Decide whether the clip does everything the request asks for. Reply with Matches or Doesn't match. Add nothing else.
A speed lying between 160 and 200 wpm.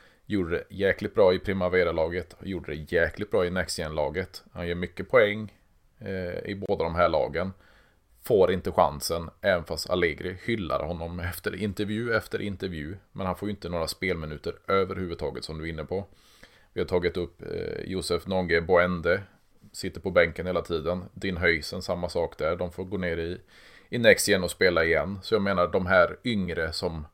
Matches